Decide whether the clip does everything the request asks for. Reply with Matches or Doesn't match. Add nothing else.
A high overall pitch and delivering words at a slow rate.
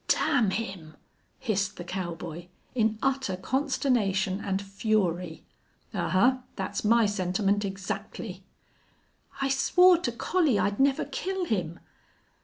Matches